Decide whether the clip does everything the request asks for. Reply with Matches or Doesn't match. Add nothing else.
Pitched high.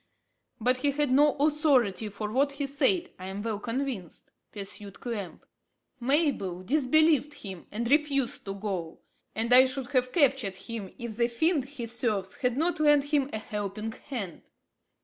Matches